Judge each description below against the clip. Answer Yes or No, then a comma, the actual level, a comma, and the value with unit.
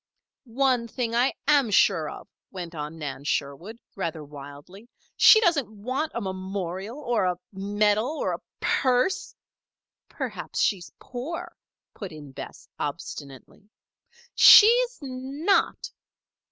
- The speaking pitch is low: No, high, 210 Hz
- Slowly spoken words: Yes, slow, 120 wpm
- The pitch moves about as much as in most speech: No, wide, 7.4 semitones